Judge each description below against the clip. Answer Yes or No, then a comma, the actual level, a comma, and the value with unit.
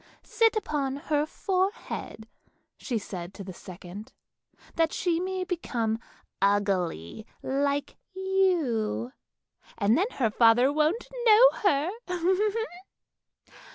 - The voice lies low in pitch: No, very high, 285 Hz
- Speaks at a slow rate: Yes, slow, 105 wpm